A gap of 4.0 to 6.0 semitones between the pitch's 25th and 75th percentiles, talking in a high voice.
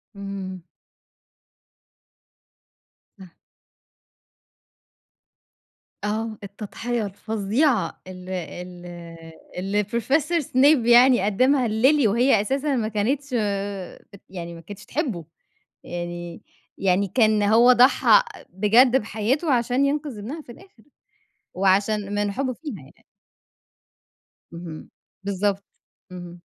Yes: average, 4.7 semitones; high, 210 Hz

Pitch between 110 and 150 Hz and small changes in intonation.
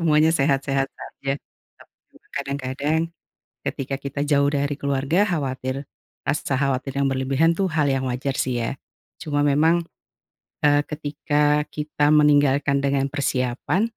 Yes: medium, 140 Hz; narrow, 1.6 semitones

